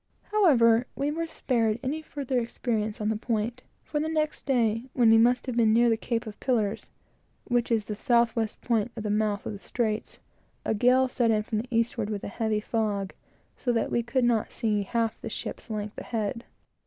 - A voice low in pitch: No, high, 230 Hz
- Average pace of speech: No, fast, 210 wpm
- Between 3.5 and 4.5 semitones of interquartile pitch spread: No, narrow, 2.4 semitones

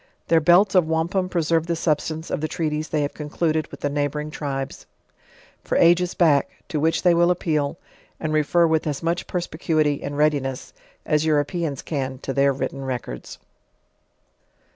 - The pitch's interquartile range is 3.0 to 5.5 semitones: No, narrow, 2.5 semitones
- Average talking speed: Yes, average, 165 wpm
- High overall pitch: No, medium, 155 Hz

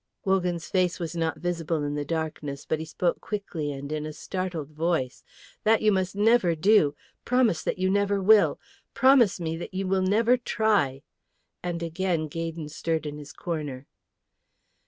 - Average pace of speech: Yes, average, 165 wpm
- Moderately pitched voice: Yes, medium, 170 Hz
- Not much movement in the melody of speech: No, average, 3.9 semitones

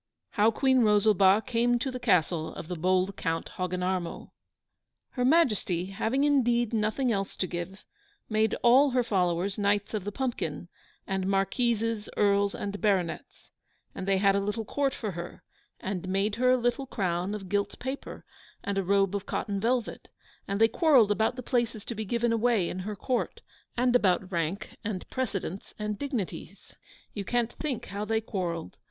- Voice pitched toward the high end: Yes, high, 205 Hz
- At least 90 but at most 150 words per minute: No, average, 170 wpm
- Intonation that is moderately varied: Yes, average, 3.9 semitones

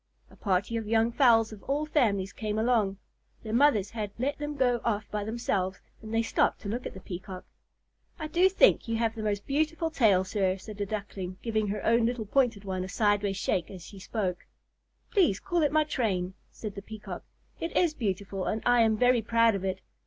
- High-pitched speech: Yes, high, 220 Hz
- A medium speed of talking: No, fast, 210 wpm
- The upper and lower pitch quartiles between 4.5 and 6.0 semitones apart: No, average, 3.6 semitones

